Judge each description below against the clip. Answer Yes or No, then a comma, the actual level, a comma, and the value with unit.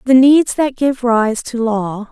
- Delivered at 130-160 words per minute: No, average, 200 wpm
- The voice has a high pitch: Yes, high, 245 Hz